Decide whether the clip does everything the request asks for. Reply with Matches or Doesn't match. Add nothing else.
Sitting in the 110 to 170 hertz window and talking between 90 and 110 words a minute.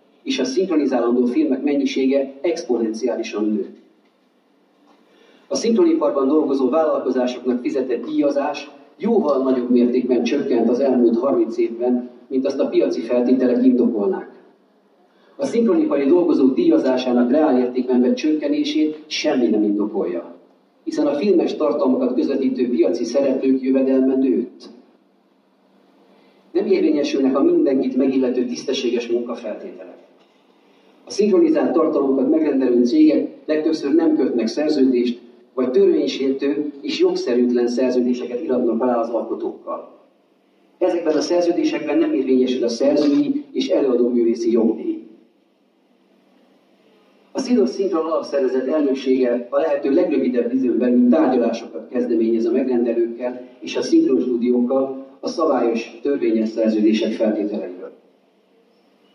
Matches